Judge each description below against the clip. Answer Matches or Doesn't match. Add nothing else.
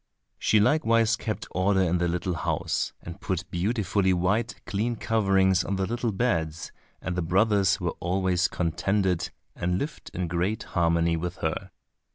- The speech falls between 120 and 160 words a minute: Matches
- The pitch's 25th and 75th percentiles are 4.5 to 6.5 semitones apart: Doesn't match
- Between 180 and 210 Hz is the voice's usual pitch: Doesn't match